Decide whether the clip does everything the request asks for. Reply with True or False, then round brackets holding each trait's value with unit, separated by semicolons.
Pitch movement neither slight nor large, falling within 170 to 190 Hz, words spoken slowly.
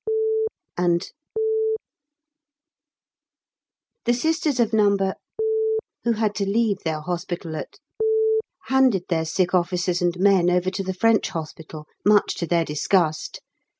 True (3.7 semitones; 185 Hz; 115 wpm)